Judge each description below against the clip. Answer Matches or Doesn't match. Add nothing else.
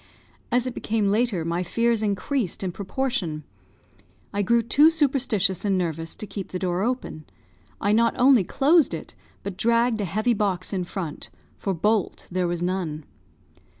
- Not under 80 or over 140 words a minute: Doesn't match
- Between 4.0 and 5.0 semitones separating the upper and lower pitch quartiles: Matches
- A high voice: Matches